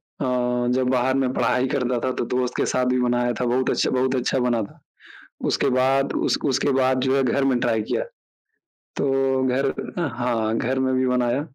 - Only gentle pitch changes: Yes, narrow, 1.3 semitones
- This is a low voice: Yes, low, 130 Hz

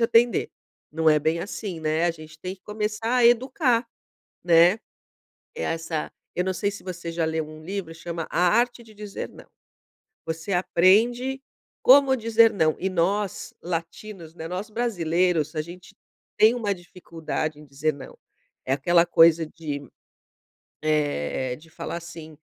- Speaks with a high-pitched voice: No, medium, 175 Hz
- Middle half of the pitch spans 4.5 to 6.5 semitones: Yes, average, 4.8 semitones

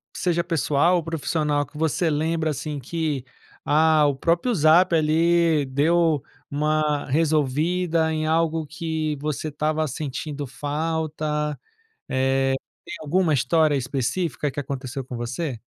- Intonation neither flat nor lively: No, narrow, 2.3 semitones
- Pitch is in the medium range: Yes, medium, 155 Hz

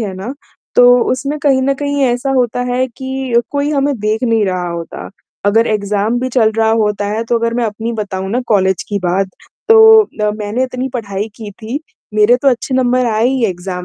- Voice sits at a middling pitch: No, high, 230 Hz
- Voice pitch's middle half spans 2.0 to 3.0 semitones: No, average, 3.9 semitones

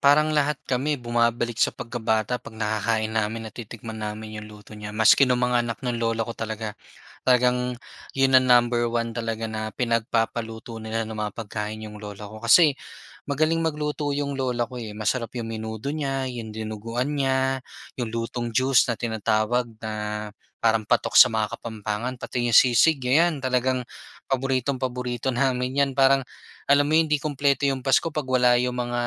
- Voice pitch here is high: No, low, 120 Hz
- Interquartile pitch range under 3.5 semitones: Yes, average, 3.1 semitones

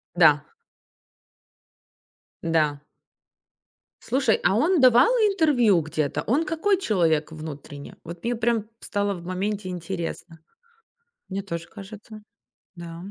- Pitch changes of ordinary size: No, wide, 6.3 semitones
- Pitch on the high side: Yes, high, 195 Hz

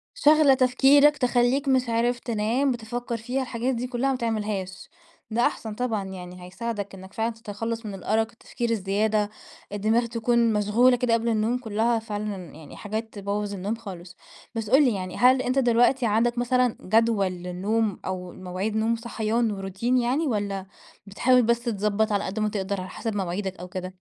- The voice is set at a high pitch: Yes, high, 225 Hz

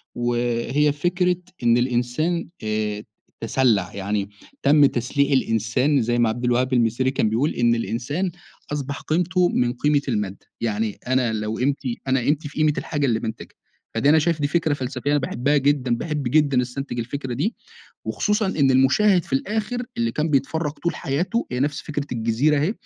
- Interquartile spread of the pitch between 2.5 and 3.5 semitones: No, average, 4.0 semitones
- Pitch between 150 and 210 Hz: No, low, 135 Hz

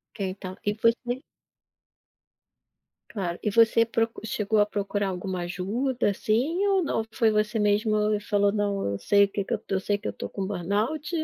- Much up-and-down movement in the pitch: No, narrow, 2.5 semitones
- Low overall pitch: No, high, 210 Hz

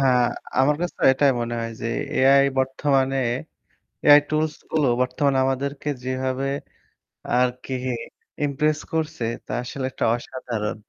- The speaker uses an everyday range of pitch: No, narrow, 2.2 semitones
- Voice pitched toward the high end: No, low, 135 Hz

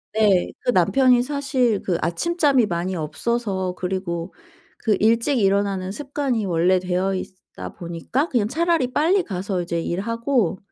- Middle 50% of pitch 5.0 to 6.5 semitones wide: Yes, wide, 5.6 semitones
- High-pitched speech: Yes, high, 205 Hz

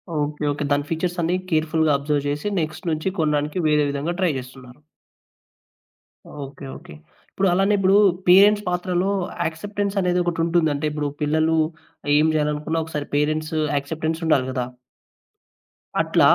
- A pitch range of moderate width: Yes, average, 3.0 semitones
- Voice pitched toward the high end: No, medium, 155 Hz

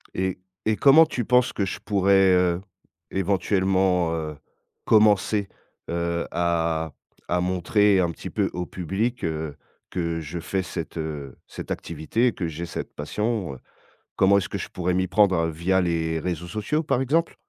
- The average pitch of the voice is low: Yes, very low, 90 Hz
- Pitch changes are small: No, average, 3.3 semitones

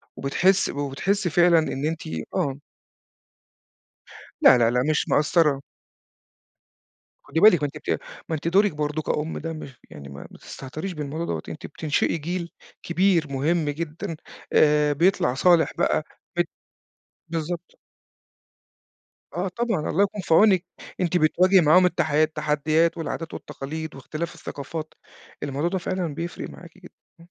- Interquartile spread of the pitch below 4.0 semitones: Yes, average, 2.9 semitones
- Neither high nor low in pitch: Yes, medium, 160 Hz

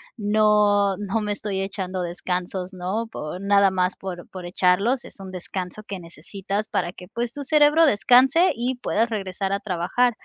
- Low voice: No, high, 200 Hz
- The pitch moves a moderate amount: Yes, average, 3.3 semitones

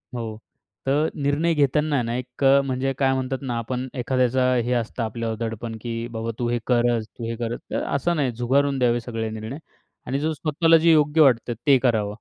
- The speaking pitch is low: Yes, low, 125 Hz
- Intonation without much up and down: No, average, 3.1 semitones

